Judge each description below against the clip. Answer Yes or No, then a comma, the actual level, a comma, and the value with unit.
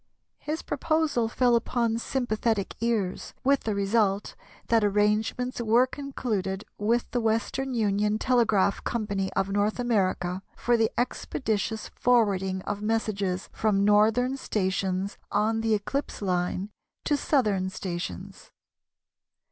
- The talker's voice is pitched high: Yes, high, 215 Hz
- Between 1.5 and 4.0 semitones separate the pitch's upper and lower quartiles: Yes, average, 3.3 semitones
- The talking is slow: Yes, slow, 115 wpm